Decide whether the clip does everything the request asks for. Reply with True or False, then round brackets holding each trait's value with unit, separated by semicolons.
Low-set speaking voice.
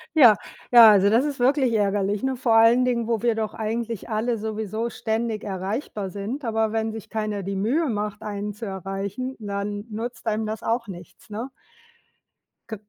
False (220 Hz)